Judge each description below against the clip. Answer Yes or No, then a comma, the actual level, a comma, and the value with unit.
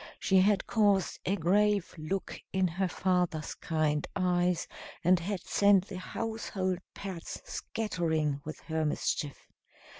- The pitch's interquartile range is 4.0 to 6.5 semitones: No, average, 3.2 semitones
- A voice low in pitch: No, medium, 185 Hz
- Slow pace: Yes, slow, 125 wpm